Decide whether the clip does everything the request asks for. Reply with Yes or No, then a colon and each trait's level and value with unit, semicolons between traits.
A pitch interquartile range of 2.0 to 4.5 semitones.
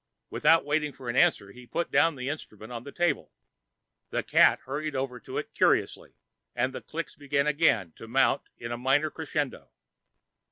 Yes: average, 3.7 semitones